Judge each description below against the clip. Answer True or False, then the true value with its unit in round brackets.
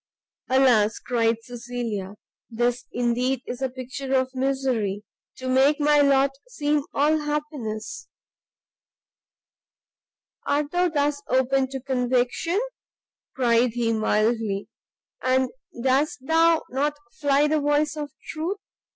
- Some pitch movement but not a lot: True (3.3 semitones)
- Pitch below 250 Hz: False (260 Hz)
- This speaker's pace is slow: True (110 wpm)